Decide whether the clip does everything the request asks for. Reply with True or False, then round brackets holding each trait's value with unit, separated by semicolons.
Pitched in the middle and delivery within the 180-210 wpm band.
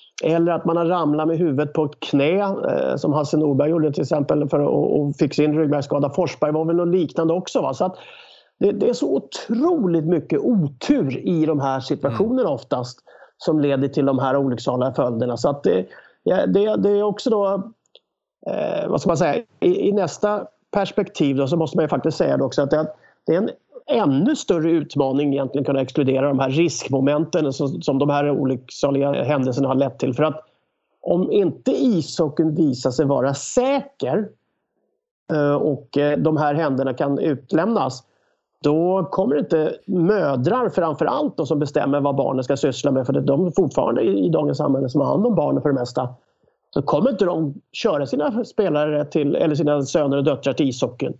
True (150 Hz; 185 wpm)